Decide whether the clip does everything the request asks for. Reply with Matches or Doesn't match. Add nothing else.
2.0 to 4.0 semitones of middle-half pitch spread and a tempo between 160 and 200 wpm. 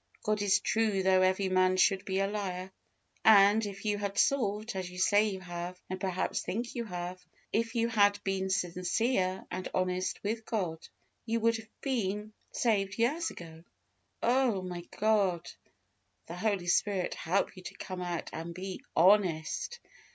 Matches